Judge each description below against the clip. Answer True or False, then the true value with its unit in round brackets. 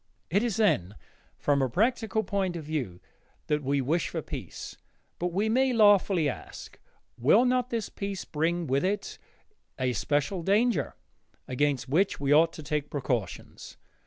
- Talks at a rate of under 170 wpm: True (155 wpm)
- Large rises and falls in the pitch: True (6.5 semitones)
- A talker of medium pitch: True (165 Hz)